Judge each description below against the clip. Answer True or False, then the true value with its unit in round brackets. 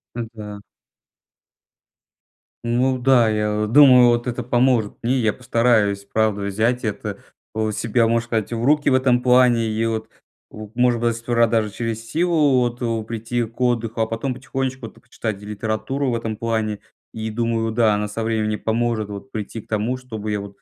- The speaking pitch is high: False (115 Hz)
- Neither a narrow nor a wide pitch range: False (2.2 semitones)